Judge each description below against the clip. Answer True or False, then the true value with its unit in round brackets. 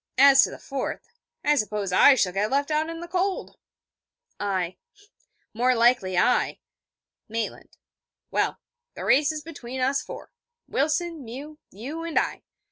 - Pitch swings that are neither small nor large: False (5.7 semitones)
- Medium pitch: False (270 Hz)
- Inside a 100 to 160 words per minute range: True (145 wpm)